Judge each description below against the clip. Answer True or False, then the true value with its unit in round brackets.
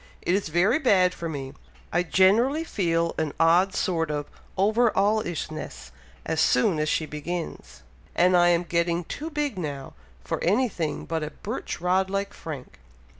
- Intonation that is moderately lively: True (3.7 semitones)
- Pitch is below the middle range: False (175 Hz)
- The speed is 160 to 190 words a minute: True (175 wpm)